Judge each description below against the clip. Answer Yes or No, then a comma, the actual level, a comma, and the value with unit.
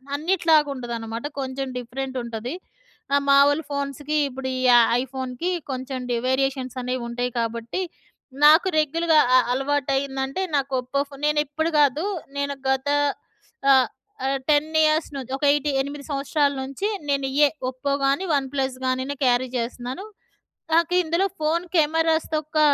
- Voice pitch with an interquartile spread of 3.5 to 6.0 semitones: No, average, 2.7 semitones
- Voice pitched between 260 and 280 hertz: Yes, very high, 275 Hz